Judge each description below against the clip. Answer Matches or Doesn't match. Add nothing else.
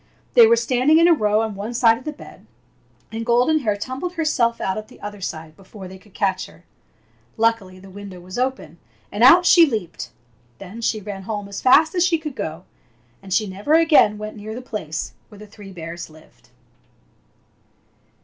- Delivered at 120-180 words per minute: Doesn't match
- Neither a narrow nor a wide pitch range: Matches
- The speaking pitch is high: Matches